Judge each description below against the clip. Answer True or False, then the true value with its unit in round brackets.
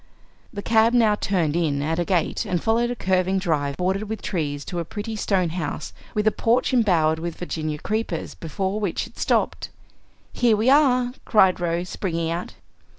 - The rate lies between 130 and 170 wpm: False (180 wpm)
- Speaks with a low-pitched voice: False (185 Hz)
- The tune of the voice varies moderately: True (4.7 semitones)